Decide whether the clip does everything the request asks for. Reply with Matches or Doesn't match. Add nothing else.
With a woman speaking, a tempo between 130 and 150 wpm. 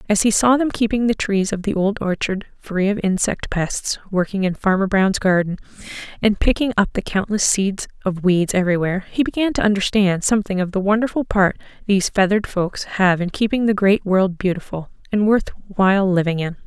Doesn't match